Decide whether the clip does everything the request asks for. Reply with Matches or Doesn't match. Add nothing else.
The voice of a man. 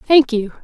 Doesn't match